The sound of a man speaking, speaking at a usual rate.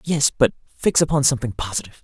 Yes: male; average, 175 wpm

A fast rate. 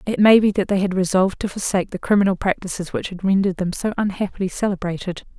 Yes: fast, 210 wpm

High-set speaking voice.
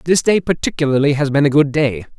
No: medium, 145 Hz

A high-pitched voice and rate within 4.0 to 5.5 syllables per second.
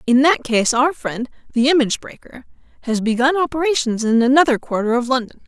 No: very high, 260 Hz; 5.8 syllables/s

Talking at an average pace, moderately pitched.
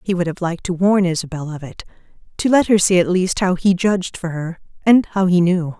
No: fast, 240 wpm; medium, 180 Hz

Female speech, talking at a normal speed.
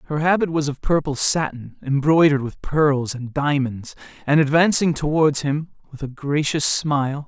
No: male; average, 155 wpm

